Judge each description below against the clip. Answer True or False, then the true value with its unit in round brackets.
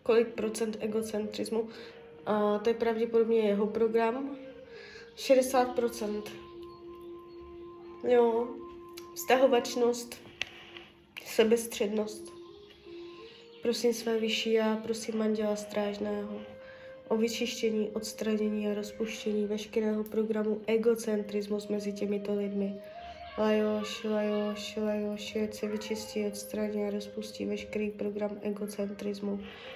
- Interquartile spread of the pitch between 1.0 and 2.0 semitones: False (2.5 semitones)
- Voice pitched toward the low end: False (220 Hz)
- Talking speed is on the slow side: True (85 wpm)